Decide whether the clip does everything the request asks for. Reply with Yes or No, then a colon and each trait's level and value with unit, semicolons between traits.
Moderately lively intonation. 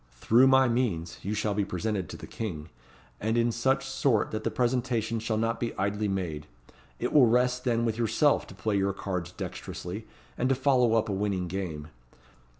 Yes: average, 3.9 semitones